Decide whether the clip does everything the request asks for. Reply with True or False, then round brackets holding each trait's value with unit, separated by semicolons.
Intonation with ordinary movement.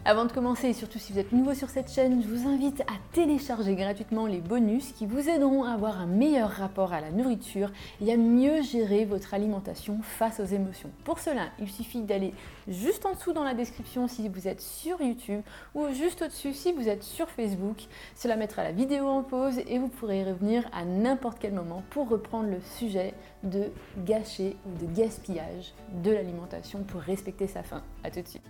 True (4.6 semitones)